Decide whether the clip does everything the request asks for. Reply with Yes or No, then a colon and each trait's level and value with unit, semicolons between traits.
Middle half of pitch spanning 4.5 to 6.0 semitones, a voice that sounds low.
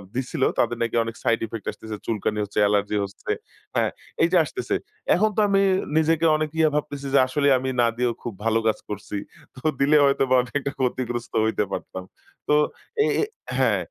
Yes: average, 4.9 semitones; low, 125 Hz